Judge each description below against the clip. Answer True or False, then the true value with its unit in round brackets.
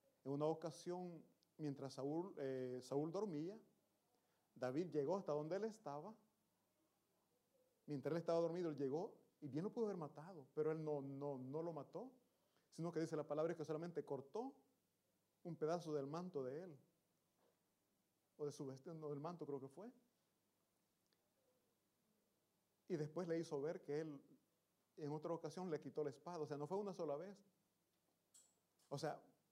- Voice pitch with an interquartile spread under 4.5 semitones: True (3.6 semitones)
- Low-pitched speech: False (155 Hz)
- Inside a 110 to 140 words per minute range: False (165 wpm)